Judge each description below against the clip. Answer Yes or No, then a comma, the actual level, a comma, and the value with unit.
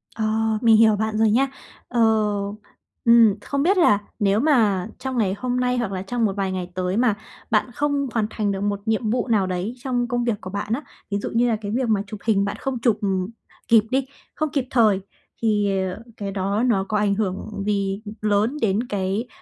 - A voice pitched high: Yes, high, 215 Hz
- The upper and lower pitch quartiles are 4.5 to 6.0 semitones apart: No, average, 3.4 semitones